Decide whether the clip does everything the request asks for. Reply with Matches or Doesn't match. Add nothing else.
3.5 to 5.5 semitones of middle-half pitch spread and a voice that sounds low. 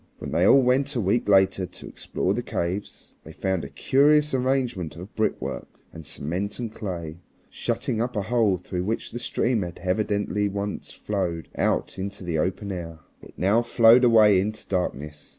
Matches